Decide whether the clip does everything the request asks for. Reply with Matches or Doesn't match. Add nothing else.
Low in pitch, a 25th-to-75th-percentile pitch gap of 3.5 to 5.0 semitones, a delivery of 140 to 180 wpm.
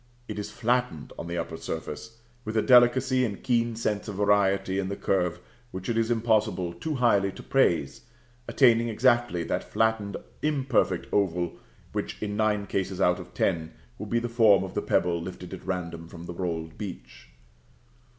Matches